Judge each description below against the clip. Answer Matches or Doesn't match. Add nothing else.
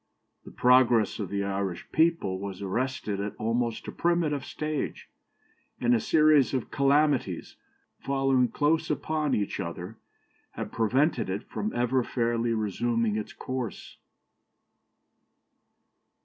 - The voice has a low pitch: Matches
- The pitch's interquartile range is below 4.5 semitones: Doesn't match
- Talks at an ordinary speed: Doesn't match